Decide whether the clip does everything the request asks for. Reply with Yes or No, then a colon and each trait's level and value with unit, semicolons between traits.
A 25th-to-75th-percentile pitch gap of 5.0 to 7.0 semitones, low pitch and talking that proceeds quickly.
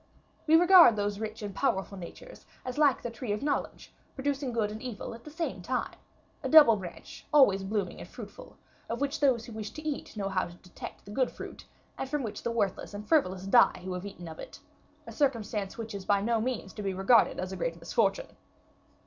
No: wide, 5.4 semitones; high, 220 Hz; fast, 215 wpm